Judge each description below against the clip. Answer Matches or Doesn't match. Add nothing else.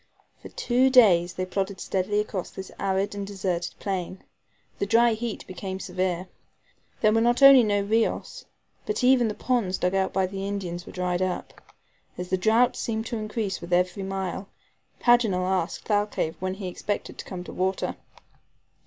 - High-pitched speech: Matches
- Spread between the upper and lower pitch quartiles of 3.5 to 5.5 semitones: Doesn't match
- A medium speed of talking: Matches